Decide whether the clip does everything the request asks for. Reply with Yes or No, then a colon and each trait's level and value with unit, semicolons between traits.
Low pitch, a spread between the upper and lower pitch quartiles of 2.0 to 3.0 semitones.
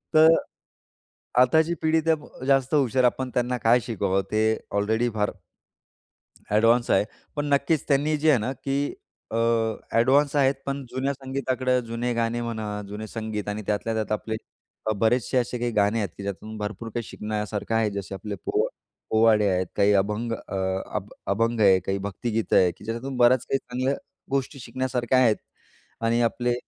No: low, 115 Hz; average, 3.4 semitones